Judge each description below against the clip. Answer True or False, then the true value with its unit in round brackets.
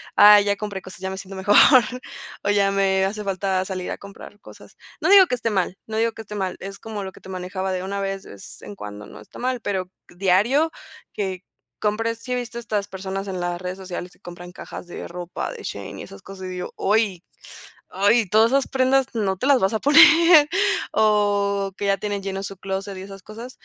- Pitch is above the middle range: True (195 Hz)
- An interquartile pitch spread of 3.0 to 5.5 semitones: False (2.5 semitones)